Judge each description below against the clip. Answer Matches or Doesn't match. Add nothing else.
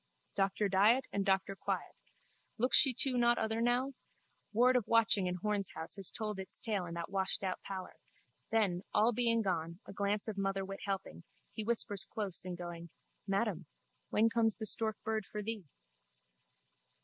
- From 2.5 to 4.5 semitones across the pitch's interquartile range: Matches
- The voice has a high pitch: Matches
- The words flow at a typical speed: Matches